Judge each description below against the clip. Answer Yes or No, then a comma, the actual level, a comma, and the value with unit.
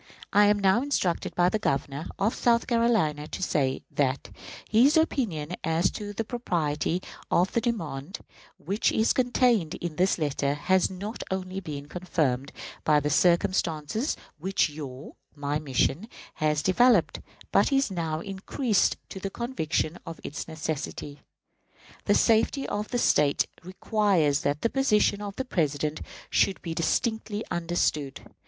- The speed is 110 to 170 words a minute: Yes, average, 145 wpm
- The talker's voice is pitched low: No, medium, 180 Hz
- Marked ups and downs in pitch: Yes, wide, 6.2 semitones